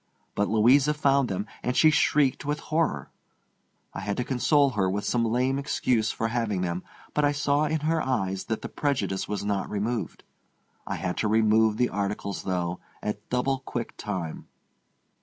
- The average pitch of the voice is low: Yes, low, 115 Hz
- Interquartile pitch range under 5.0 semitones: No, average, 5.3 semitones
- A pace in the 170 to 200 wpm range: Yes, average, 175 wpm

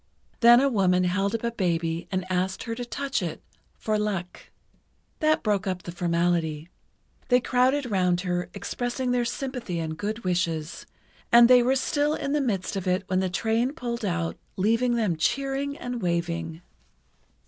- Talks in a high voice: Yes, high, 200 Hz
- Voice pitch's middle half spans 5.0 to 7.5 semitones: Yes, wide, 5.6 semitones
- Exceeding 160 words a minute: Yes, average, 170 wpm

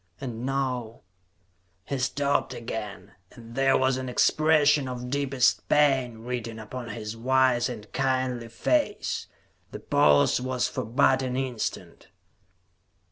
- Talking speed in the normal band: No, slow, 130 wpm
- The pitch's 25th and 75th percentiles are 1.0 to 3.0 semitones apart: Yes, average, 2.7 semitones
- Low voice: Yes, low, 125 Hz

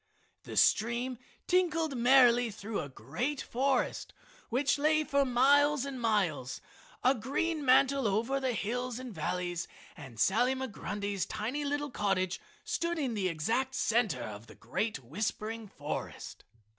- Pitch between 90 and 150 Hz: No, high, 240 Hz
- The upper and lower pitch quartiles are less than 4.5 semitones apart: No, average, 5.3 semitones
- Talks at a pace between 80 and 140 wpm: Yes, slow, 135 wpm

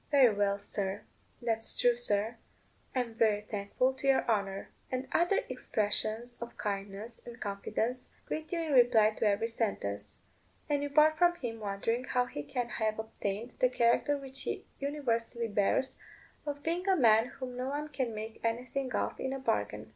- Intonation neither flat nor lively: Yes, average, 3.7 semitones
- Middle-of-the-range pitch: No, high, 235 Hz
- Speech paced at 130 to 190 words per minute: Yes, average, 170 wpm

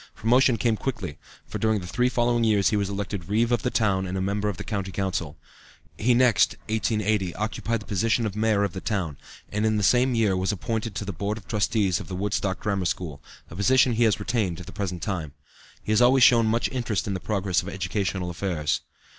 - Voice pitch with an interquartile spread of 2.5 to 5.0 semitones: Yes, average, 3.1 semitones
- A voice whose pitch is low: Yes, low, 105 Hz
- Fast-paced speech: Yes, fast, 225 wpm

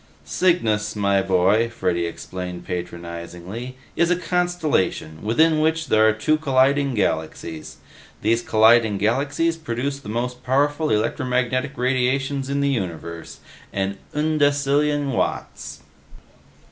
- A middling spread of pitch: No, wide, 6.4 semitones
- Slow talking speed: Yes, slow, 110 wpm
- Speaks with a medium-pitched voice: No, low, 125 Hz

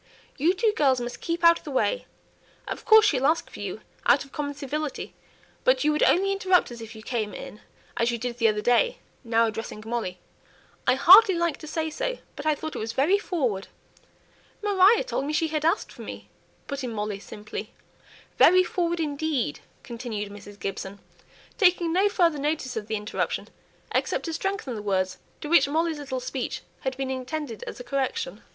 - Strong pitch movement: Yes, wide, 6.6 semitones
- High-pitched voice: Yes, very high, 285 Hz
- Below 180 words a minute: No, average, 195 wpm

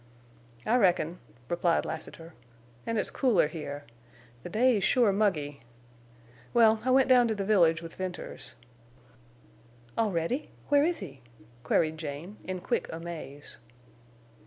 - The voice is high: No, medium, 180 Hz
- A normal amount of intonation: No, wide, 5.8 semitones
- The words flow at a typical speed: No, slow, 125 wpm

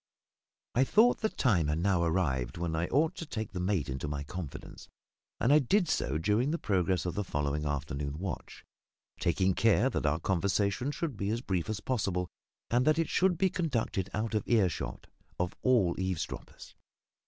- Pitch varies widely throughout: Yes, wide, 6.9 semitones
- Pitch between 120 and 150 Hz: No, very low, 95 Hz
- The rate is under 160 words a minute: No, average, 180 wpm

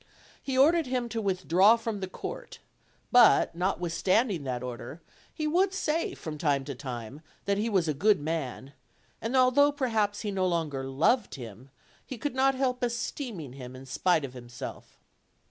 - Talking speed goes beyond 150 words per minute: Yes, average, 170 wpm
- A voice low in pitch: No, high, 190 Hz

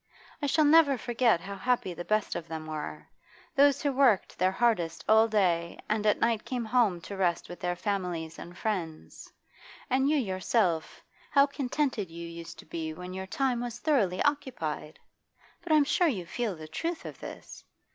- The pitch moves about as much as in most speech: No, wide, 6.9 semitones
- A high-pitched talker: Yes, high, 210 Hz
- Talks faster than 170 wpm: Yes, average, 180 wpm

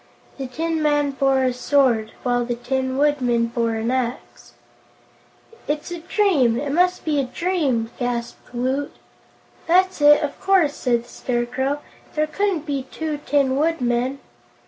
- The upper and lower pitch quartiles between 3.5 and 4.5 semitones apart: Yes, average, 3.9 semitones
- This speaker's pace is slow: No, average, 145 wpm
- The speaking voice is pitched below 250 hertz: No, very high, 270 Hz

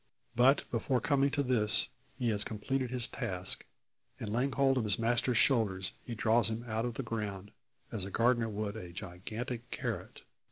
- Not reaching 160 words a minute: No, average, 175 wpm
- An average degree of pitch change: Yes, average, 3.1 semitones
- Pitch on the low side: Yes, low, 115 Hz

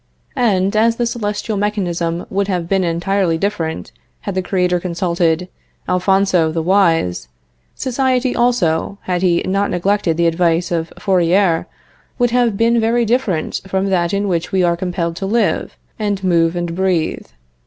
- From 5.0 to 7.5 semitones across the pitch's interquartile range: No, average, 3.2 semitones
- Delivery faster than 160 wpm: No, average, 155 wpm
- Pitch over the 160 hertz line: Yes, medium, 185 Hz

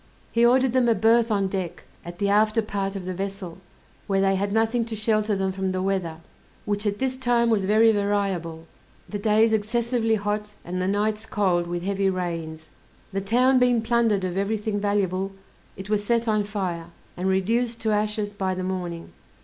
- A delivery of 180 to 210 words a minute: Yes, average, 190 wpm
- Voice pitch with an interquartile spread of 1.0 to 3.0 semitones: Yes, average, 2.7 semitones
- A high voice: Yes, high, 205 Hz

